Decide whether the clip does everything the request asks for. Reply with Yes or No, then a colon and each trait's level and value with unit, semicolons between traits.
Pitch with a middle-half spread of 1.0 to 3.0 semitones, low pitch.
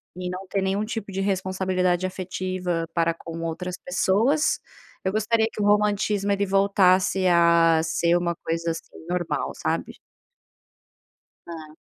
No: average, 2.7 semitones; medium, 185 Hz